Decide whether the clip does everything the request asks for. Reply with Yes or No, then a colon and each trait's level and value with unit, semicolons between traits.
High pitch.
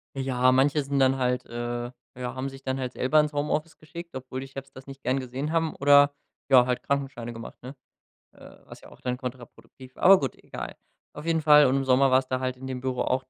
No: low, 130 Hz